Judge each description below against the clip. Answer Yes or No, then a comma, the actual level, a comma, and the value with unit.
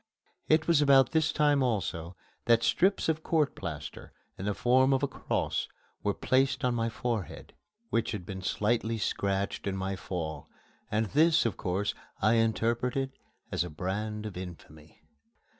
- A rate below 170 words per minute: Yes, average, 160 wpm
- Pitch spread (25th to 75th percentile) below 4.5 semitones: No, wide, 5.6 semitones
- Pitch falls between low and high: No, low, 115 Hz